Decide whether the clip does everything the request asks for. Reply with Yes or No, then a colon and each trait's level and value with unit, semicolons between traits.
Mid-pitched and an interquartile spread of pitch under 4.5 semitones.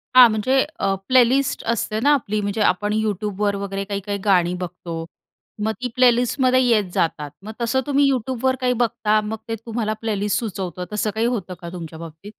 No: high, 215 Hz; average, 3.8 semitones